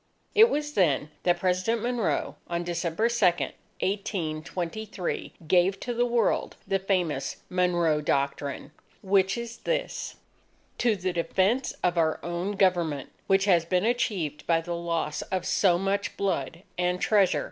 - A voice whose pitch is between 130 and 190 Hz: Yes, medium, 185 Hz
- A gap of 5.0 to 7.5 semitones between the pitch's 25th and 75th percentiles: No, average, 3.4 semitones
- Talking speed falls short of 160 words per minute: Yes, average, 140 wpm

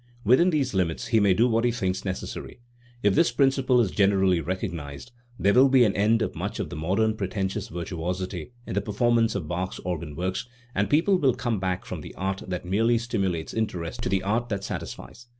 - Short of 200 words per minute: No, fast, 205 wpm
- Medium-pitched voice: No, low, 100 Hz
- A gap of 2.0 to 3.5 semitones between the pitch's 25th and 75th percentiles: No, average, 4.2 semitones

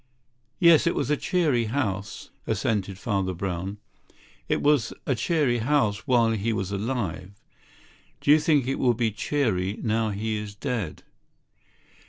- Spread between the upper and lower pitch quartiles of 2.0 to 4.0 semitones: No, average, 4.9 semitones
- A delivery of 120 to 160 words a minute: Yes, average, 145 wpm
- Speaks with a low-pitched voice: Yes, low, 110 Hz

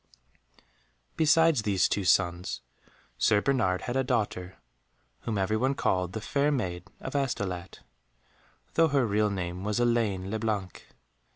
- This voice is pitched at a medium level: No, low, 105 Hz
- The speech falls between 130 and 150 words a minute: Yes, slow, 135 wpm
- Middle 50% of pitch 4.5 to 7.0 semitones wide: Yes, wide, 5.6 semitones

